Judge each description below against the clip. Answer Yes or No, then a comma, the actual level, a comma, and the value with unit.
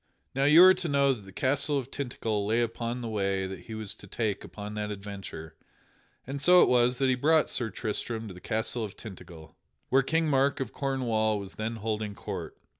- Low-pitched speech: Yes, low, 115 Hz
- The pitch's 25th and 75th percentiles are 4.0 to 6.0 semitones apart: Yes, average, 4.5 semitones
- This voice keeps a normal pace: No, fast, 210 wpm